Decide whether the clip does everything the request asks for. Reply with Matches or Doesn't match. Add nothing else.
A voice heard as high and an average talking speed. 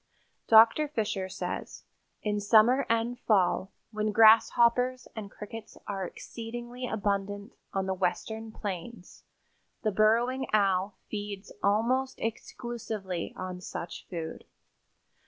Doesn't match